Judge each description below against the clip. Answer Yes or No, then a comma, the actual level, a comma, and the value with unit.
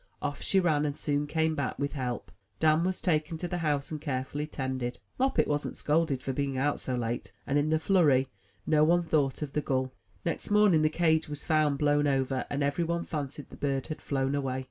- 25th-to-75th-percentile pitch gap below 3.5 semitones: Yes, narrow, 2.6 semitones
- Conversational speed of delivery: No, fast, 215 wpm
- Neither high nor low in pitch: Yes, medium, 145 Hz